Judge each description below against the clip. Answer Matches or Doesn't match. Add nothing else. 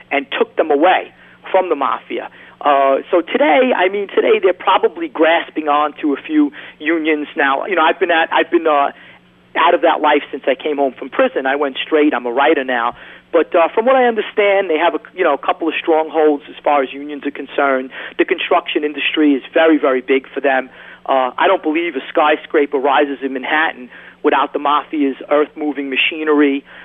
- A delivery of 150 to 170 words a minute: Doesn't match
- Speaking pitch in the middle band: Matches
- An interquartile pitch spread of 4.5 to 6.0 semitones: Doesn't match